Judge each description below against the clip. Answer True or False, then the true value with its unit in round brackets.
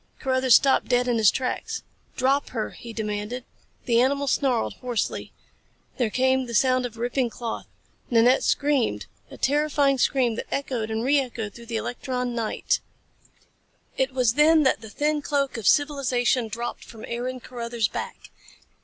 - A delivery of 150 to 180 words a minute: True (155 wpm)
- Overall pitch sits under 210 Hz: False (250 Hz)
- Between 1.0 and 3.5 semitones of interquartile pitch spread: True (2.6 semitones)